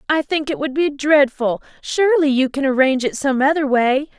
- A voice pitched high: Yes, very high, 280 Hz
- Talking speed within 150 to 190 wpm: No, average, 200 wpm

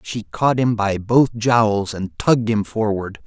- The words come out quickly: No, average, 185 wpm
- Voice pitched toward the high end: No, low, 110 Hz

